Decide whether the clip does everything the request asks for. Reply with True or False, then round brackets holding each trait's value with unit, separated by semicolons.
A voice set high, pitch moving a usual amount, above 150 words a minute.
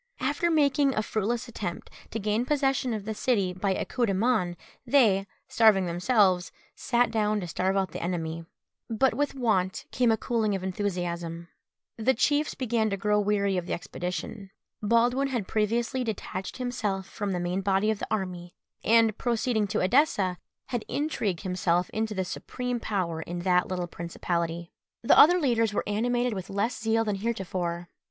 True (210 Hz; 4.4 semitones; 170 wpm)